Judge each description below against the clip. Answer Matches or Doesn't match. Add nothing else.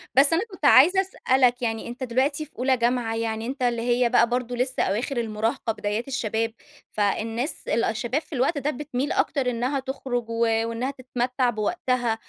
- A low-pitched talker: Doesn't match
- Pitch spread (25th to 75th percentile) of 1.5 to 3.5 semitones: Matches